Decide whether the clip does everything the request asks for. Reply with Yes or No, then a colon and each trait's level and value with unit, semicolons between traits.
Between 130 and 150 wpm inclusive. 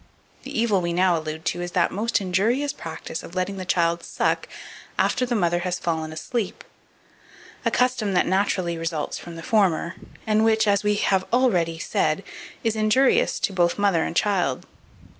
No: average, 175 wpm